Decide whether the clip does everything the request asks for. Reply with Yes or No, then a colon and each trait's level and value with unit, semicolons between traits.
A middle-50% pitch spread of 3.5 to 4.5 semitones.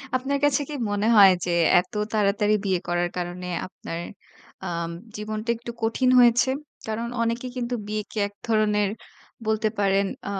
No: average, 3.0 semitones